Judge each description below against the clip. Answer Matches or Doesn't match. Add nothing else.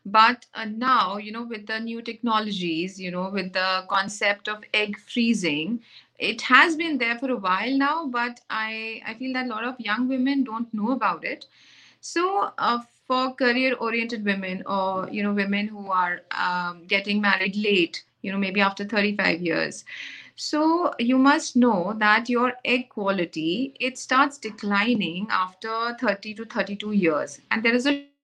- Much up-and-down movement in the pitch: Doesn't match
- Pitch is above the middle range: Matches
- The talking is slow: Doesn't match